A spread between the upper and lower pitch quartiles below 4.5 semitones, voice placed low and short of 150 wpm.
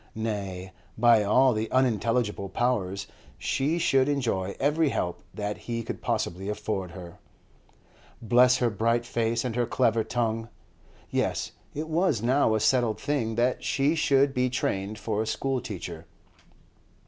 Yes: average, 3.6 semitones; low, 115 Hz; average, 140 wpm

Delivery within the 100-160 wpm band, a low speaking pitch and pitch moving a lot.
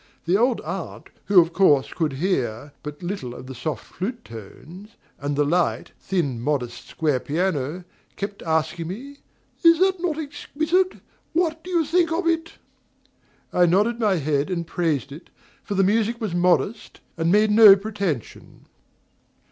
No: average, 155 wpm; medium, 185 Hz; wide, 7.5 semitones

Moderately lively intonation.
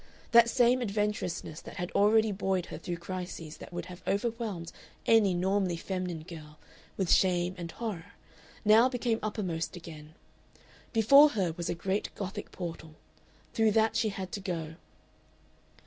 Yes: average, 4.1 semitones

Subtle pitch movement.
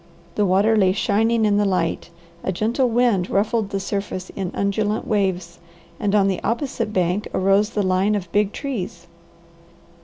Yes: narrow, 2.3 semitones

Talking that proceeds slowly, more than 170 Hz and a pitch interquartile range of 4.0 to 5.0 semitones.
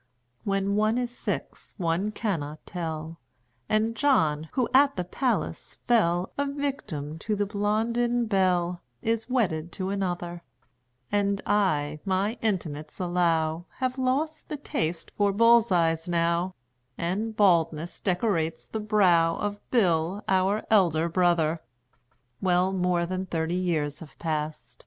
Yes: slow, 130 wpm; medium, 185 Hz; average, 4.4 semitones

